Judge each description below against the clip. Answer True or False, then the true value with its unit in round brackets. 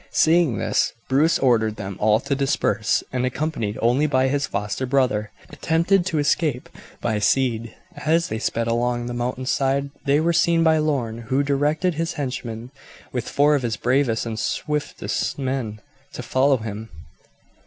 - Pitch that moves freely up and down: False (4.3 semitones)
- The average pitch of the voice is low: True (130 Hz)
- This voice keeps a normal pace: True (160 wpm)